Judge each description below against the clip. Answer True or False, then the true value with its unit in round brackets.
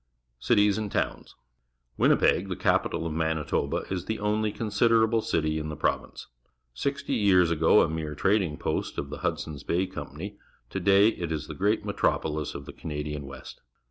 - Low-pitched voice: True (85 Hz)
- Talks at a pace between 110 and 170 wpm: False (185 wpm)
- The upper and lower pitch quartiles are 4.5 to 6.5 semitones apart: True (5.4 semitones)